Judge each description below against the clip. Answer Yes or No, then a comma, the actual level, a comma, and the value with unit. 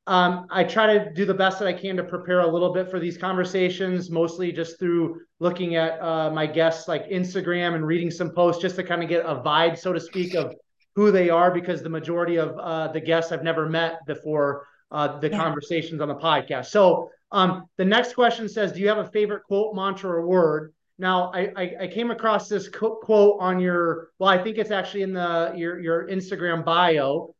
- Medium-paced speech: No, fast, 215 wpm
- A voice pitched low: No, medium, 180 Hz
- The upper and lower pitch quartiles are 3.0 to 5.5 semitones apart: No, narrow, 2.5 semitones